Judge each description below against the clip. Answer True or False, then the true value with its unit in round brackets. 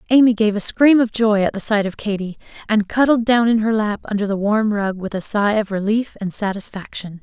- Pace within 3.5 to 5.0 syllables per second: False (5.4 syllables/s)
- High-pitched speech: True (210 Hz)